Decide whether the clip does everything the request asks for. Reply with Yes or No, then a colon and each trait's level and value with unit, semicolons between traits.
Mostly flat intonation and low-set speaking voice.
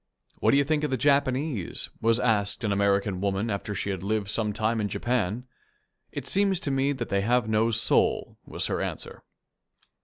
No: average, 4.5 semitones; low, 110 Hz